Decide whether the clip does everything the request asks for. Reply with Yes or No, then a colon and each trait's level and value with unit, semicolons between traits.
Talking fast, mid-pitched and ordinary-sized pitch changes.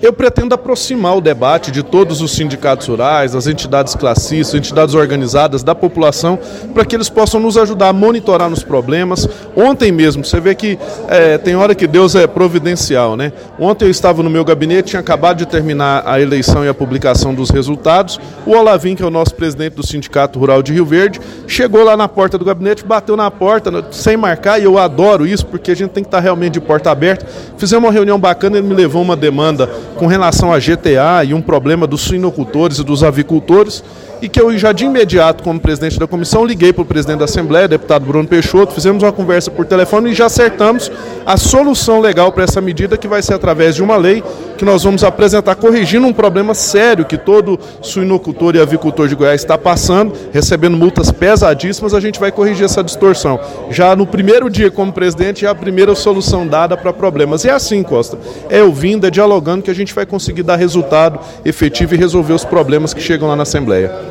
Yes: fast, 205 wpm; medium, 180 Hz; average, 4.5 semitones